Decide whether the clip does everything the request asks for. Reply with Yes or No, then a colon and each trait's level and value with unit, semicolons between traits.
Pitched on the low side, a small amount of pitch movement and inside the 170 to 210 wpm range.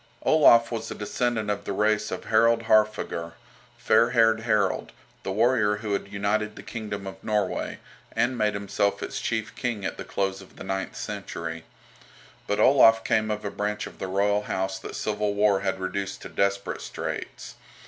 Yes: low, 105 Hz; narrow, 2.0 semitones; average, 180 wpm